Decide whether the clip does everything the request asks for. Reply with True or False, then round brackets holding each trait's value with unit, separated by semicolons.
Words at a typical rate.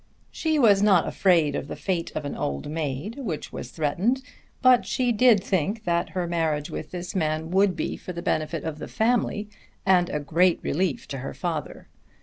True (190 wpm)